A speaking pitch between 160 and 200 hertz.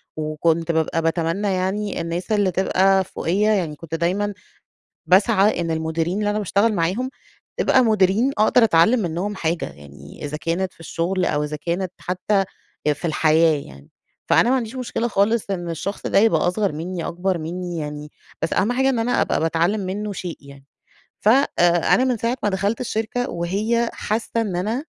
Yes: medium, 185 Hz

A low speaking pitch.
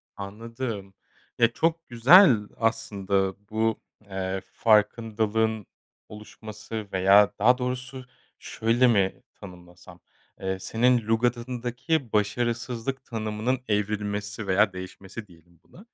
Yes: low, 110 Hz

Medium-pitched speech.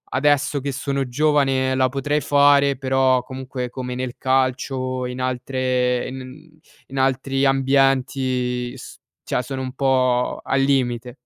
No: low, 130 Hz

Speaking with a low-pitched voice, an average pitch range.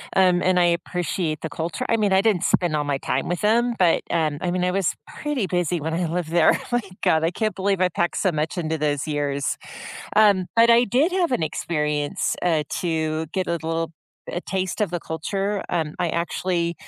No: medium, 175 Hz; average, 3.3 semitones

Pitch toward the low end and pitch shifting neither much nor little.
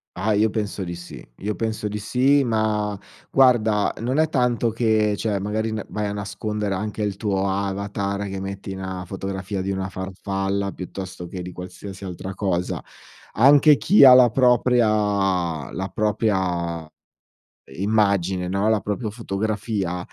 No: low, 100 Hz; narrow, 2.3 semitones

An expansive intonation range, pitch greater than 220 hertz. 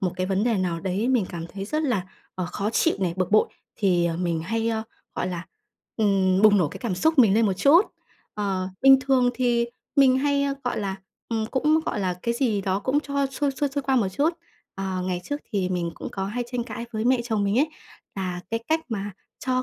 No: wide, 5.7 semitones; high, 215 Hz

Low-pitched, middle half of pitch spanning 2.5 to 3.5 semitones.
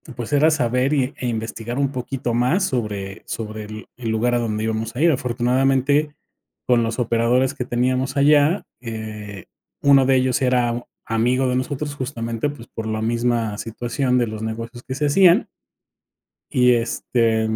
Yes: low, 125 Hz; average, 2.8 semitones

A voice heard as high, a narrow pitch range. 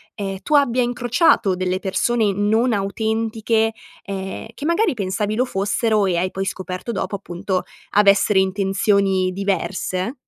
No: high, 200 Hz; average, 3.0 semitones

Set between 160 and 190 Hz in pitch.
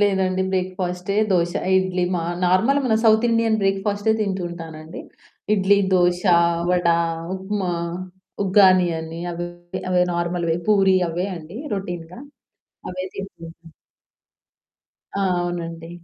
Yes: medium, 185 Hz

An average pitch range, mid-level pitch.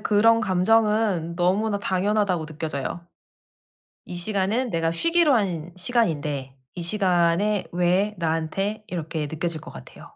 Yes: average, 4.3 semitones; medium, 180 Hz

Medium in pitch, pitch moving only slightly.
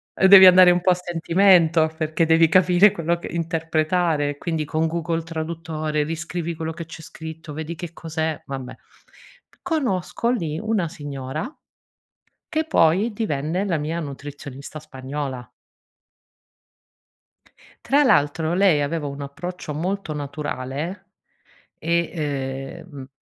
No: medium, 160 Hz; average, 3.0 semitones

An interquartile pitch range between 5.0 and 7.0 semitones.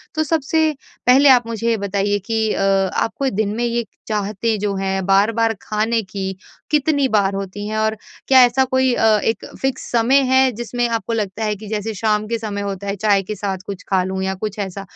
No: average, 3.0 semitones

